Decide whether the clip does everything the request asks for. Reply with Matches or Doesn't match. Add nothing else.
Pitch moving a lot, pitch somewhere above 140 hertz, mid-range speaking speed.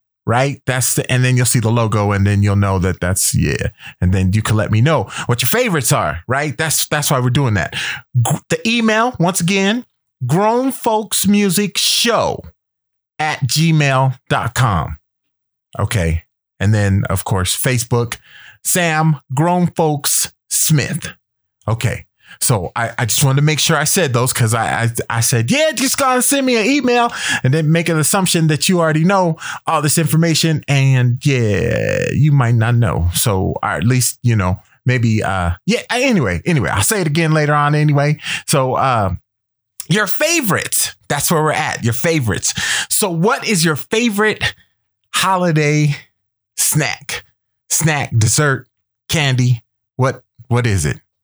Doesn't match